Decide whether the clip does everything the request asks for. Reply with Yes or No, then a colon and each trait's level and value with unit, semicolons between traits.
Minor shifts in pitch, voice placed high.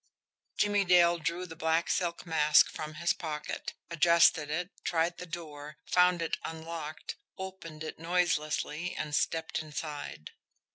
No: narrow, 2.1 semitones; medium, 165 Hz